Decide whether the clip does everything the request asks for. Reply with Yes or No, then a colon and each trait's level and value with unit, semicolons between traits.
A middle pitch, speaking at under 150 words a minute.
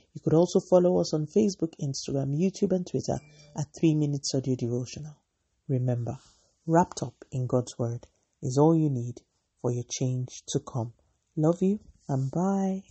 No: medium, 145 Hz; average, 165 wpm